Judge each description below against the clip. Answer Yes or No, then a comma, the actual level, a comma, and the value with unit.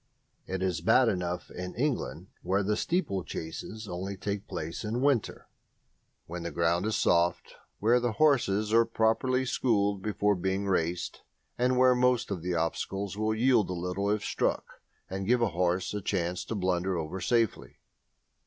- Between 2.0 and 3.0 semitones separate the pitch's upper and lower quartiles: No, average, 4.1 semitones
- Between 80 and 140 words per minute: No, average, 160 wpm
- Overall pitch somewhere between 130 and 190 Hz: No, low, 100 Hz